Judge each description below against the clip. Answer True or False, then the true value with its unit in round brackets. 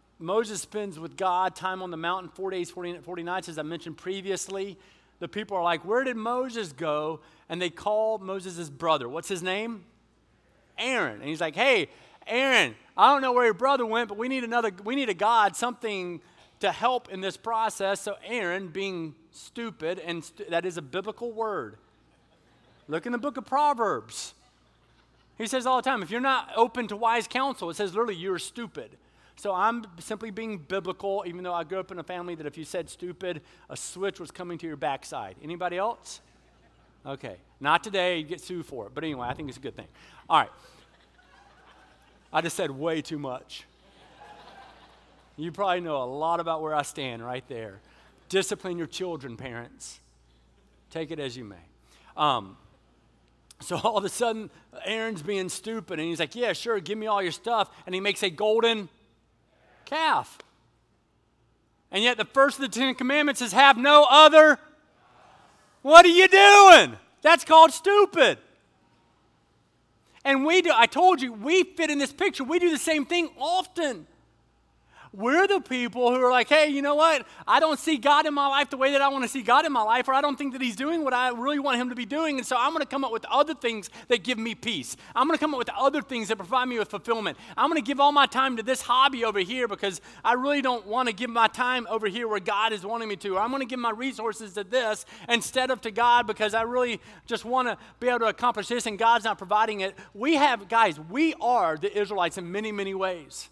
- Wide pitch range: True (6.3 semitones)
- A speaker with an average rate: False (210 wpm)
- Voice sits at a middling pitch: False (220 Hz)